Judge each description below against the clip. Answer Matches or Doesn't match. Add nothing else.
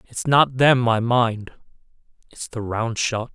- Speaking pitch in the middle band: Doesn't match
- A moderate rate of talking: Matches